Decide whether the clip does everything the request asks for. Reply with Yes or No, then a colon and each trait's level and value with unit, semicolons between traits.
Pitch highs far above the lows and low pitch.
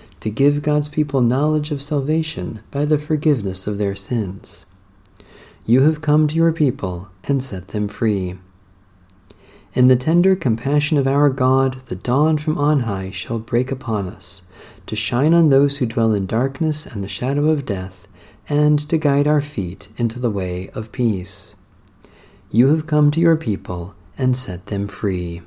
Yes: wide, 6.8 semitones; low, 115 Hz